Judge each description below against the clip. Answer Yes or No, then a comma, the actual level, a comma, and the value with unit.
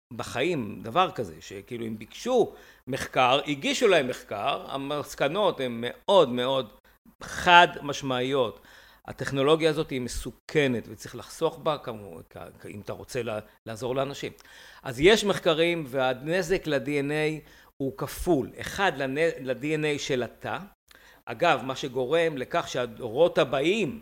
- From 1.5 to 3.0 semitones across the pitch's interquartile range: No, average, 4.2 semitones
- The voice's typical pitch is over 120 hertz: Yes, medium, 140 Hz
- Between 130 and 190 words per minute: No, average, 120 wpm